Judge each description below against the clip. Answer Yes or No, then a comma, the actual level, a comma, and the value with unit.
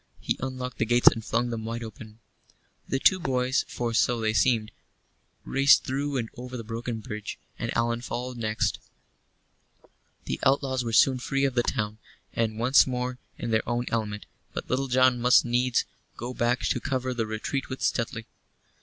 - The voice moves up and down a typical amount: No, narrow, 2.1 semitones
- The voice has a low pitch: Yes, low, 120 Hz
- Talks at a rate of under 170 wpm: No, average, 175 wpm